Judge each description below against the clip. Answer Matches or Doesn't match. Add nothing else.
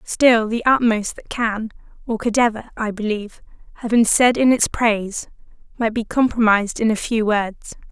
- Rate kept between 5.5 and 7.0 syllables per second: Doesn't match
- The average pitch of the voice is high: Matches